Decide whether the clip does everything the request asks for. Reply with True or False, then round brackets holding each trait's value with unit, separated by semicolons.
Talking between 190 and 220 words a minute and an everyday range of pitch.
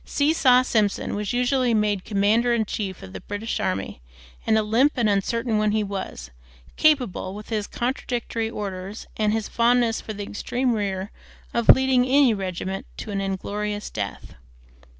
False (160 wpm; 3.3 semitones)